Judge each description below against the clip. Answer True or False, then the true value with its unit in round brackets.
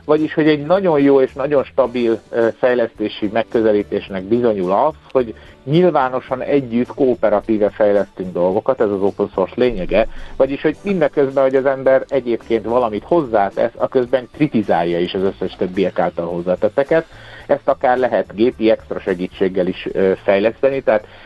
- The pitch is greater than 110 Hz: True (120 Hz)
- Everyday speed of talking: True (140 wpm)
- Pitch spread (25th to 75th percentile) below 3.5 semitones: False (4.8 semitones)